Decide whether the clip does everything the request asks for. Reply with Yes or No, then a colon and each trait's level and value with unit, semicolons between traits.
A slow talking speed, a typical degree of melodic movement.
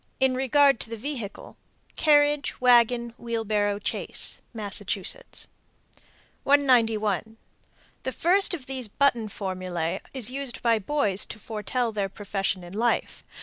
Yes: slow, 120 wpm; average, 4.4 semitones